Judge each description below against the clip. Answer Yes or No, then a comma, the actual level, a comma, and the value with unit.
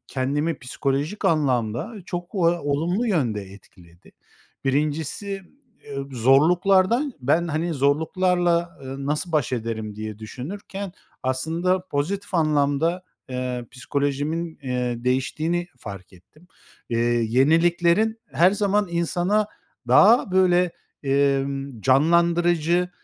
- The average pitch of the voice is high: No, medium, 155 Hz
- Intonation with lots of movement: No, average, 5.0 semitones